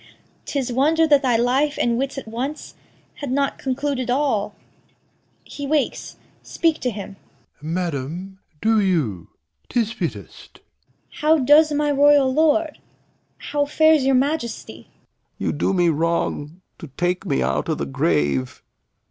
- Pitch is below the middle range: No, very high, 250 Hz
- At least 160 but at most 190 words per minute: No, average, 145 wpm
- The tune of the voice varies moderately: No, wide, 8.5 semitones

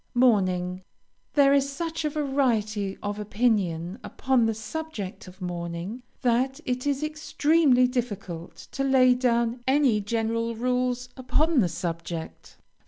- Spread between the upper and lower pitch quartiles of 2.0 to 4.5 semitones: No, average, 5.0 semitones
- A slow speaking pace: Yes, slow, 125 wpm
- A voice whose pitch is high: Yes, high, 240 Hz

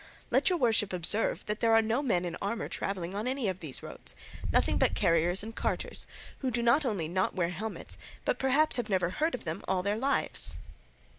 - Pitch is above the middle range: Yes, high, 210 Hz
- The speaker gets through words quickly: Yes, fast, 210 wpm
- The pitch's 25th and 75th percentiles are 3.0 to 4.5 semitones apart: No, average, 4.9 semitones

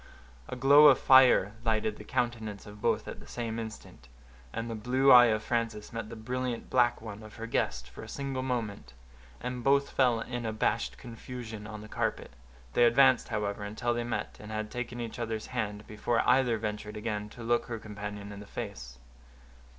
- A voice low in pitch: Yes, low, 115 Hz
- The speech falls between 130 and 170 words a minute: No, average, 190 wpm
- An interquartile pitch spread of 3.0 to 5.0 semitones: No, narrow, 2.5 semitones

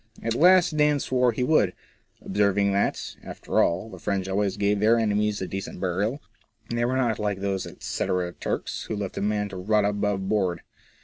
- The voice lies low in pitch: Yes, low, 105 Hz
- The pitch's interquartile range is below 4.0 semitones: Yes, average, 2.9 semitones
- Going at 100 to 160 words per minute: No, average, 185 wpm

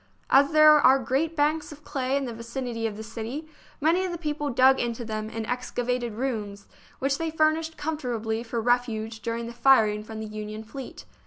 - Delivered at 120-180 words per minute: No, average, 190 wpm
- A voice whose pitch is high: Yes, high, 245 Hz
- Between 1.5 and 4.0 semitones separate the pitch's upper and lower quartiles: No, average, 4.6 semitones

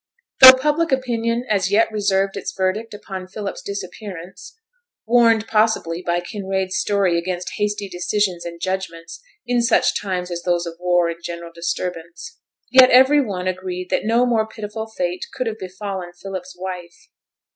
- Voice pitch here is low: No, high, 190 Hz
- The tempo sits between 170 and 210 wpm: No, average, 155 wpm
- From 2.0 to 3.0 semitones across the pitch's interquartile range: No, average, 3.7 semitones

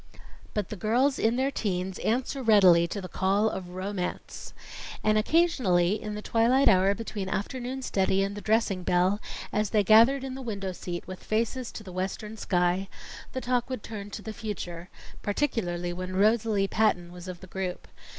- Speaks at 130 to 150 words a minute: No, average, 180 wpm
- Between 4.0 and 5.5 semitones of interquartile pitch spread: No, average, 3.5 semitones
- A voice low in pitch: No, high, 205 Hz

